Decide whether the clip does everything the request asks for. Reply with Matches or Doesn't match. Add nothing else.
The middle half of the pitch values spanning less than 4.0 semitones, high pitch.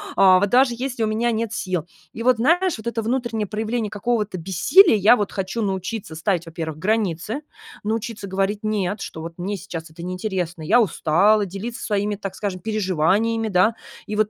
Matches